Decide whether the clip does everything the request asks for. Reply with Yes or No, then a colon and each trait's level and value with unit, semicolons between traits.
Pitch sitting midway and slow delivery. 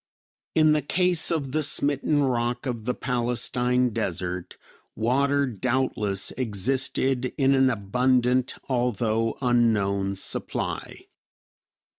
No: low, 125 Hz; slow, 100 wpm